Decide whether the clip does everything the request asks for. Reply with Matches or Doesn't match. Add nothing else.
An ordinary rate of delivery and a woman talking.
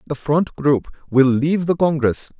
Doesn't match